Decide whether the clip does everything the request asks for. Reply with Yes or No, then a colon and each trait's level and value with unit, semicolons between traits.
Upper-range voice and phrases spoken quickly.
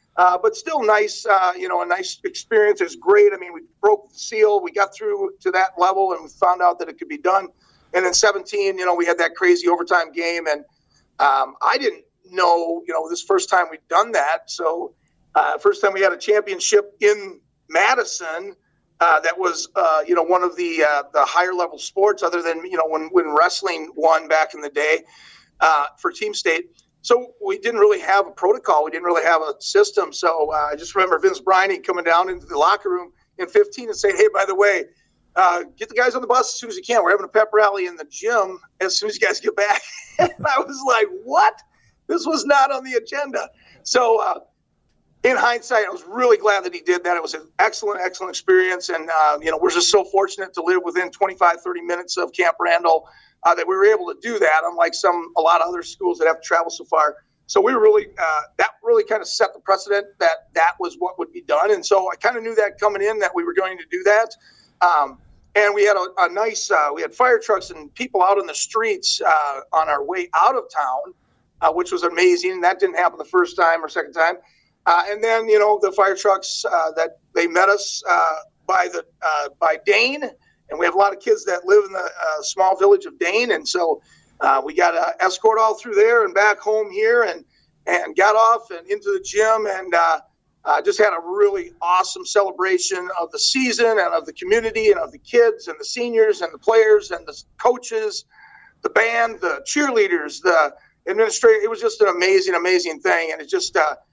Yes: high, 210 Hz; fast, 230 wpm